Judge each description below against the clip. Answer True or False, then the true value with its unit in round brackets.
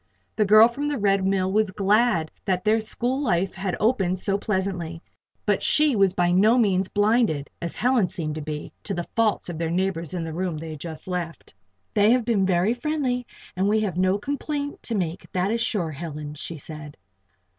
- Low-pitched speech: False (190 Hz)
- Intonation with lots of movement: False (4.4 semitones)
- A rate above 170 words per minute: True (200 wpm)